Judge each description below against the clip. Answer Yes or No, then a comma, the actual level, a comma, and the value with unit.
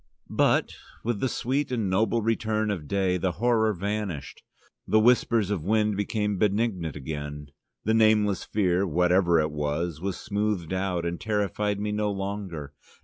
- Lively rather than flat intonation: No, average, 3.7 semitones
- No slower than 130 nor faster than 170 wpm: Yes, average, 150 wpm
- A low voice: Yes, low, 100 Hz